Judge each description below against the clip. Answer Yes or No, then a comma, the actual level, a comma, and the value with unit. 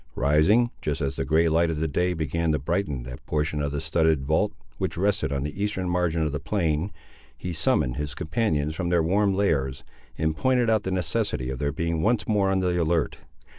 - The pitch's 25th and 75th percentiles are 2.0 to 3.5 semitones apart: No, average, 4.1 semitones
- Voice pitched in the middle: No, very low, 80 Hz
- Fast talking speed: Yes, fast, 210 wpm